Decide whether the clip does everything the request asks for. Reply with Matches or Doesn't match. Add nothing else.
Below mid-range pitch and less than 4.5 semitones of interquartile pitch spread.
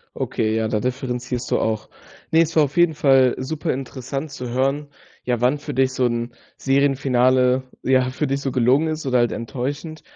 Matches